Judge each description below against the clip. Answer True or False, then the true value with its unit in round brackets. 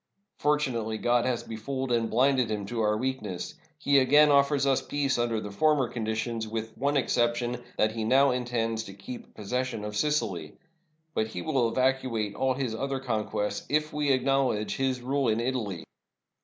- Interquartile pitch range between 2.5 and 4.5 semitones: True (3.5 semitones)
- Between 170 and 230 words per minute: True (180 wpm)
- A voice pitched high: False (120 Hz)